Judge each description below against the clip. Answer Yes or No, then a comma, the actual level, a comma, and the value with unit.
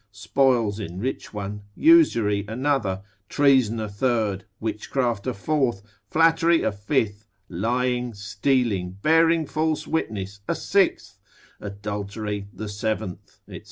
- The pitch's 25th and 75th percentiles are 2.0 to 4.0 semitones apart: No, average, 5.0 semitones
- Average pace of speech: No, slow, 110 wpm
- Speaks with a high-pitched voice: No, low, 110 Hz